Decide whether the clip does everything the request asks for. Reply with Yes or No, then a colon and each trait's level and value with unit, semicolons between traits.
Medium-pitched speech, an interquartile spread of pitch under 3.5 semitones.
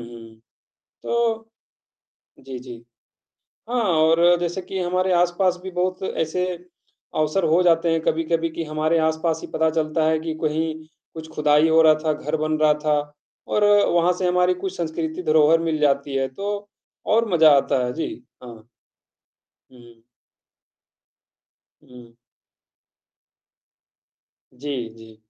Yes: medium, 160 Hz; average, 2.8 semitones